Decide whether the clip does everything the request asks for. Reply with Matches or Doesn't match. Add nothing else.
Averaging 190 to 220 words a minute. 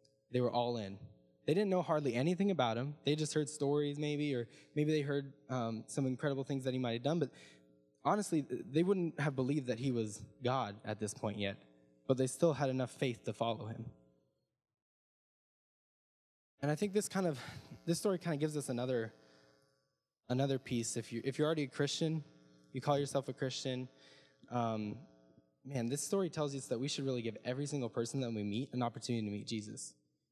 Matches